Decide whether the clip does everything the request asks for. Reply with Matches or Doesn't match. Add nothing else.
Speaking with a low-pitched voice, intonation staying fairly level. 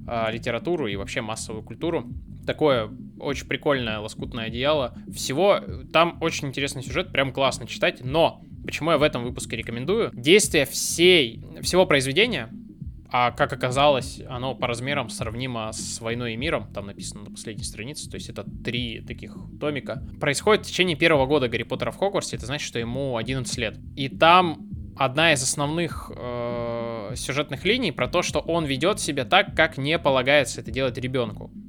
Doesn't match